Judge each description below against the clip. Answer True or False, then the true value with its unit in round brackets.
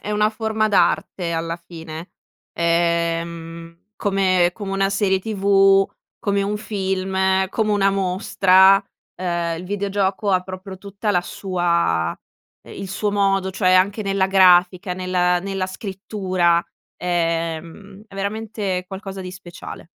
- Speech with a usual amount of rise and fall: False (2.1 semitones)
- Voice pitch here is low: False (190 Hz)